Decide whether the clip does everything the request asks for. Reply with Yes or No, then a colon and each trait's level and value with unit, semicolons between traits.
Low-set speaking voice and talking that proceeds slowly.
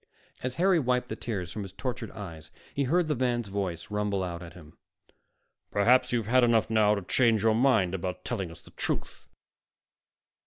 No: low, 110 Hz; average, 185 wpm